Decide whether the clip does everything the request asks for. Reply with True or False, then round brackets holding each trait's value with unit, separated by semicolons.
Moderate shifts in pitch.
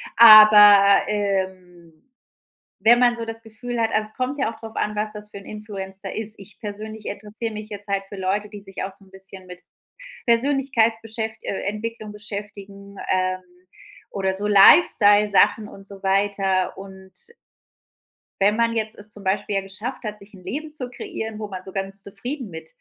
False (2.2 semitones)